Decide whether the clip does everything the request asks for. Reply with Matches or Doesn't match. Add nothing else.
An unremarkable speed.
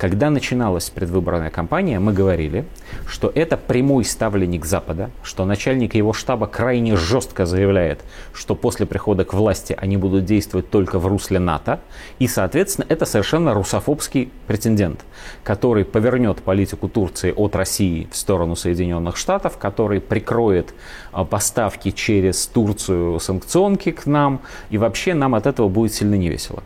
Matches